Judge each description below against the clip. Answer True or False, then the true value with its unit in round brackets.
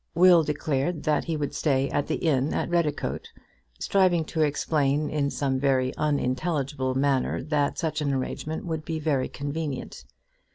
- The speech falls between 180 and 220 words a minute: False (155 wpm)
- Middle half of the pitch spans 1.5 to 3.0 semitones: True (2.6 semitones)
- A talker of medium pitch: True (150 Hz)